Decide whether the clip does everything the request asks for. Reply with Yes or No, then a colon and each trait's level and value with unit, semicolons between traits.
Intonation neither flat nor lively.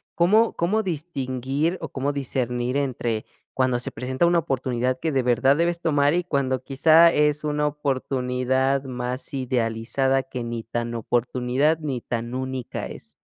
Yes: average, 3.0 semitones